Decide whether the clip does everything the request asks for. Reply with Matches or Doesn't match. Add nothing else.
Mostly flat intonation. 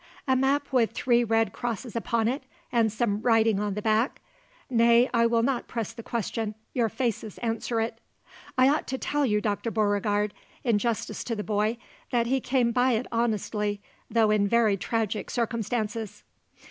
Matches